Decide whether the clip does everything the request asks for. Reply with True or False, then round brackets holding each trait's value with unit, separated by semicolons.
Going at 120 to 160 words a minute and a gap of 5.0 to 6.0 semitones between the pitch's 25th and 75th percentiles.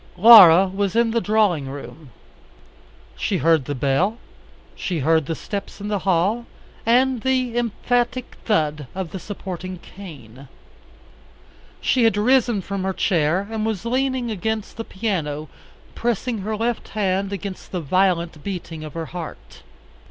True (145 wpm; 5.3 semitones)